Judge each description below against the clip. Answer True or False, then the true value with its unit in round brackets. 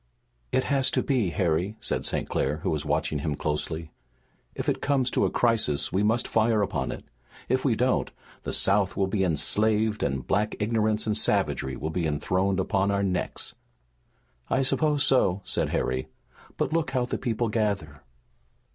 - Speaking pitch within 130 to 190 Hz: False (105 Hz)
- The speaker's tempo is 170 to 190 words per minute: True (175 wpm)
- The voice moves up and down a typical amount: False (6.1 semitones)